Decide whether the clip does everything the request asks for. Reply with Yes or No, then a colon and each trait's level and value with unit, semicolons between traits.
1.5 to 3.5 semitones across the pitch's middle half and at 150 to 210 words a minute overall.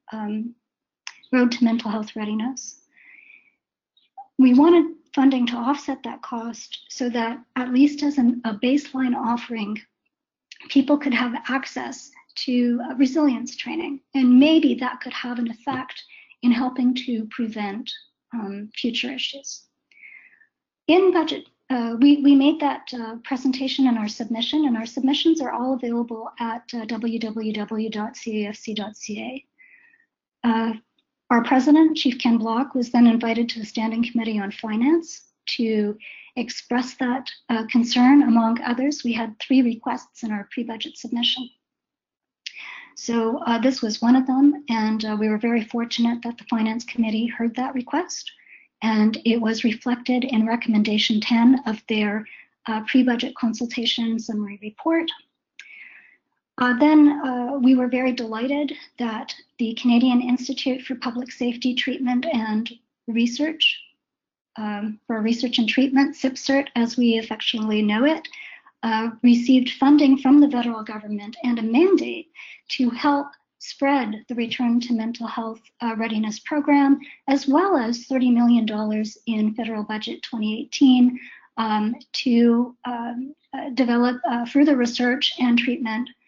No: average, 3.0 semitones; average, 140 wpm